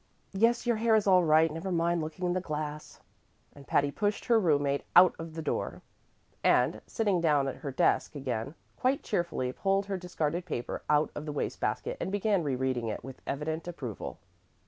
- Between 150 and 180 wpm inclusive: No, average, 195 wpm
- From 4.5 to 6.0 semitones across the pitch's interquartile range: Yes, average, 4.9 semitones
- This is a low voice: No, medium, 165 Hz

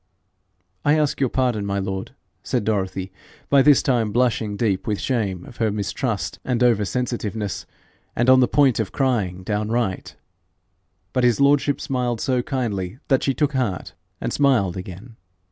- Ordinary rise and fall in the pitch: Yes, average, 4.4 semitones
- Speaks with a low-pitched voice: Yes, low, 115 Hz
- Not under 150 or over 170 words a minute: Yes, average, 160 wpm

